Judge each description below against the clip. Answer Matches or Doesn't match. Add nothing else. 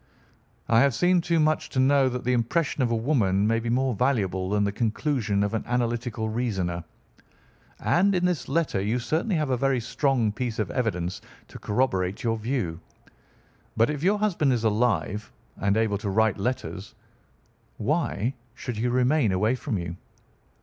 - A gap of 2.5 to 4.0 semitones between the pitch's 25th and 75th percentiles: Doesn't match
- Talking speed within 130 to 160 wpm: Doesn't match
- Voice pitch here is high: Doesn't match